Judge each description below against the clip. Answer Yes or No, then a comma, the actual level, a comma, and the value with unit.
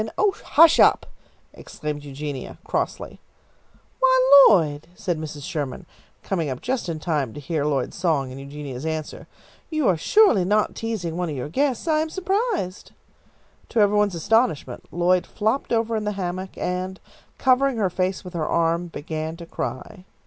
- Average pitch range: No, wide, 6.8 semitones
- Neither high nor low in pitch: Yes, medium, 180 Hz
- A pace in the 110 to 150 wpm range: No, average, 165 wpm